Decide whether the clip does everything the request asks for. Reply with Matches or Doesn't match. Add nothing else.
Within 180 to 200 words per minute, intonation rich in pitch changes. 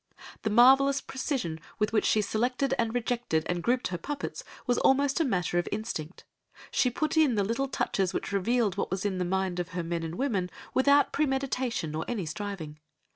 Matches